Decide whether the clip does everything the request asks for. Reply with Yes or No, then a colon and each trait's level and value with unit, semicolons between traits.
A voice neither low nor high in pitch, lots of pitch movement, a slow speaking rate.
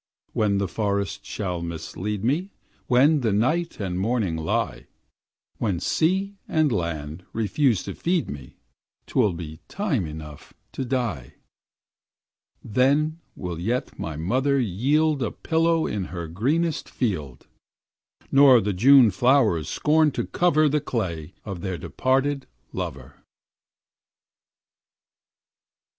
No: low, 110 Hz; wide, 8.2 semitones; slow, 120 wpm